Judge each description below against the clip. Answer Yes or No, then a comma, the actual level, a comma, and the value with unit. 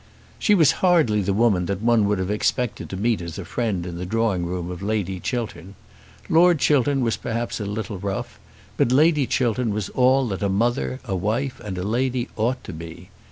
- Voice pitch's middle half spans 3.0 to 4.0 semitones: No, average, 4.7 semitones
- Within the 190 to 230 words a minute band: Yes, fast, 205 wpm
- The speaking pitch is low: Yes, low, 110 Hz